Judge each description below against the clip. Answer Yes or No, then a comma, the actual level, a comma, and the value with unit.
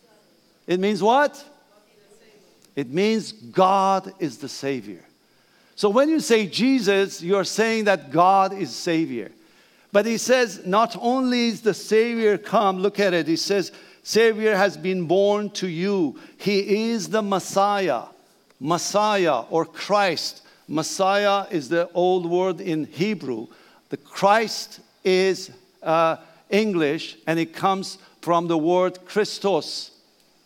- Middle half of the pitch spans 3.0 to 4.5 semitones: Yes, average, 3.3 semitones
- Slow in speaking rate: Yes, slow, 130 wpm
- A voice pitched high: Yes, high, 195 Hz